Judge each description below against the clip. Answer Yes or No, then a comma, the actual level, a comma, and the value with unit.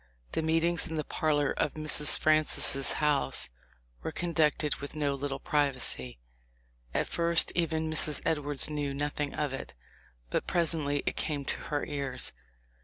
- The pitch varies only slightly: Yes, narrow, 1.8 semitones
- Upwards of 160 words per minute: No, average, 145 wpm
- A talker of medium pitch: Yes, medium, 150 Hz